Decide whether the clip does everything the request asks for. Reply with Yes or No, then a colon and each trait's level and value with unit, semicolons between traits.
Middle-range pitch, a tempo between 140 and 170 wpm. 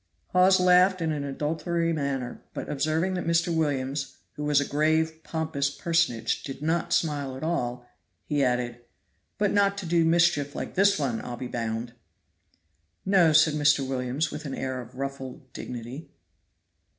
Yes: medium, 150 Hz; average, 160 wpm